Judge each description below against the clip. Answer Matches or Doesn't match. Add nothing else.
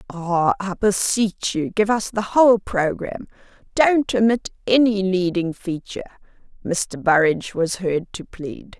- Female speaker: Matches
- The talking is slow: Matches